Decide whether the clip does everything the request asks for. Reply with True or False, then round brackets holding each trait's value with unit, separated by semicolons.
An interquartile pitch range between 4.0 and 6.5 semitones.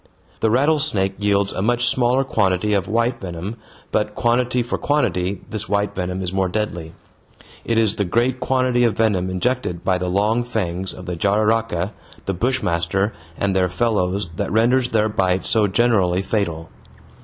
True (4.3 semitones)